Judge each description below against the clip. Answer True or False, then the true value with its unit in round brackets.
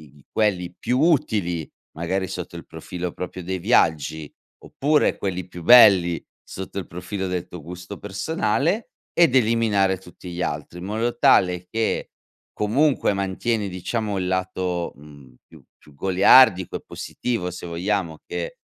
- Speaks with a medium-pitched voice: False (95 Hz)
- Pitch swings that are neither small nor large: True (3.7 semitones)